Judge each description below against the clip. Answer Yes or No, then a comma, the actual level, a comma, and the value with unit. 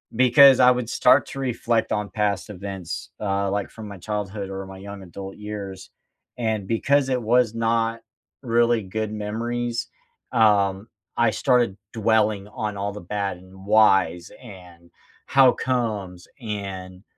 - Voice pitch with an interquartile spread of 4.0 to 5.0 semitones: No, average, 3.1 semitones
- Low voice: Yes, low, 105 Hz